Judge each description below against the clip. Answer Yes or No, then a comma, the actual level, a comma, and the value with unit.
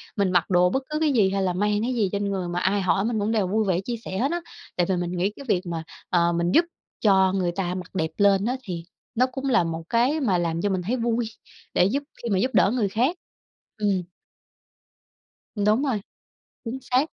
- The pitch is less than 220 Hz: Yes, high, 200 Hz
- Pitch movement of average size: Yes, average, 4.6 semitones